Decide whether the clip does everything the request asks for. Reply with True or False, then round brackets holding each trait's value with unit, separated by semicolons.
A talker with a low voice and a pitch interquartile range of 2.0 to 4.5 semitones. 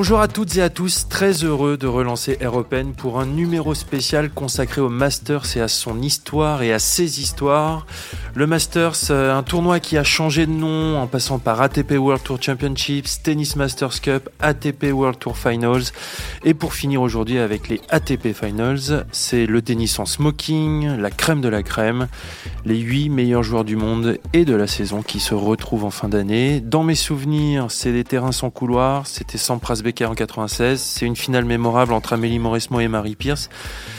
True (130 Hz; 4.2 semitones)